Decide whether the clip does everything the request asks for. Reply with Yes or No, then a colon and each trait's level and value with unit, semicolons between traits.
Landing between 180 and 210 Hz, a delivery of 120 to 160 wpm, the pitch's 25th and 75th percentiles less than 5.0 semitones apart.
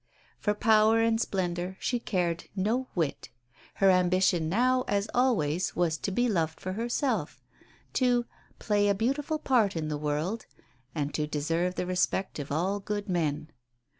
No: high, 190 Hz; average, 155 wpm; average, 5.3 semitones